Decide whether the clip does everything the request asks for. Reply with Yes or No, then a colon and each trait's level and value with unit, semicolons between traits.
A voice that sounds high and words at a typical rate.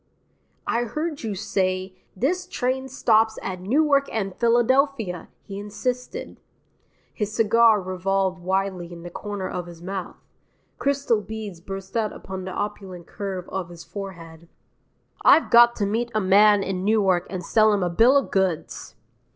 Yes: high, 200 Hz; average, 150 wpm